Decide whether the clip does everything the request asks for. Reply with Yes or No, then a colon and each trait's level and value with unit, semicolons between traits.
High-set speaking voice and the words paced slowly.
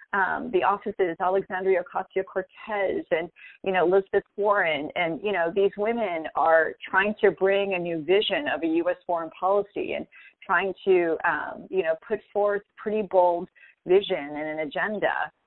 No: high, 195 Hz; average, 165 wpm